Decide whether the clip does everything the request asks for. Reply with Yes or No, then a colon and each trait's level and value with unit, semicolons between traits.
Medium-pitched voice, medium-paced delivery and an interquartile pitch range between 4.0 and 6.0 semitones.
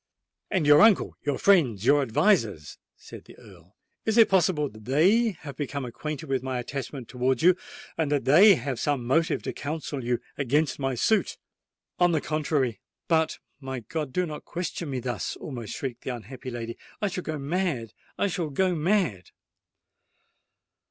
Yes: medium, 145 Hz; average, 150 wpm; average, 5.2 semitones